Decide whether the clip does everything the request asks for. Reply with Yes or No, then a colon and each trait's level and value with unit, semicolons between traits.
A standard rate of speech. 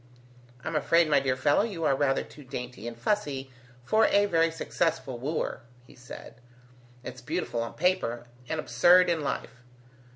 Yes: average, 160 wpm